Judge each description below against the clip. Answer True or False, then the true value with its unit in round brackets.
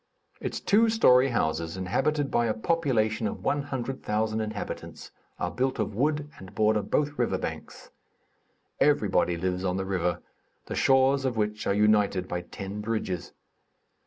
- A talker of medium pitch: False (110 Hz)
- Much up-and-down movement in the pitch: True (5.7 semitones)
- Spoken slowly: False (145 wpm)